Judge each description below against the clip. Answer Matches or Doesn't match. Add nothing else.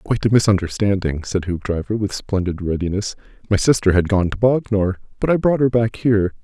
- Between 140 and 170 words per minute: Doesn't match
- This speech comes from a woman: Doesn't match